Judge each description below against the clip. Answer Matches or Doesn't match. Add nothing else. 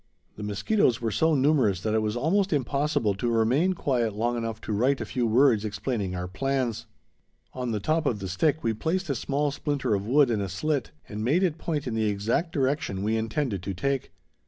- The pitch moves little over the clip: Doesn't match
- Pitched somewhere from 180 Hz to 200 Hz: Doesn't match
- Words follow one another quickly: Matches